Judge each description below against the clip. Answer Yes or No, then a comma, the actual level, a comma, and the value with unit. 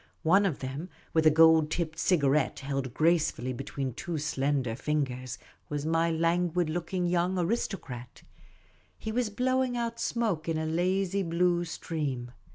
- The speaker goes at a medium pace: Yes, average, 145 wpm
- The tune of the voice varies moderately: Yes, average, 4.0 semitones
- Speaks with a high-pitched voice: No, medium, 165 Hz